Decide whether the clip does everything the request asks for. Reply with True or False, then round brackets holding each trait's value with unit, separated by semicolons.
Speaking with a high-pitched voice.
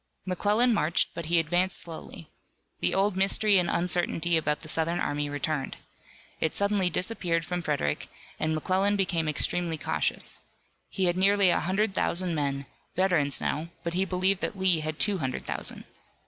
False (175 Hz)